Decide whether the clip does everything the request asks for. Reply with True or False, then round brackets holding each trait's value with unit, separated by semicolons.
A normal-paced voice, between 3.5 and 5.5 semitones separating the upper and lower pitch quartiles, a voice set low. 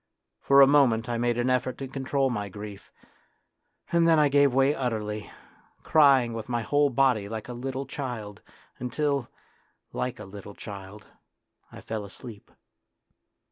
True (150 wpm; 4.2 semitones; 125 Hz)